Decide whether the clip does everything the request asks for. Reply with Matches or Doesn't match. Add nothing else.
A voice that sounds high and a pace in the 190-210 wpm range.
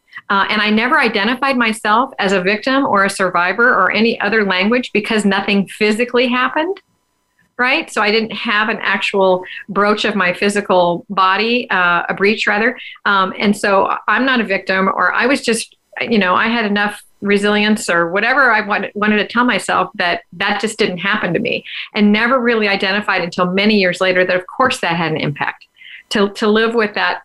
Matches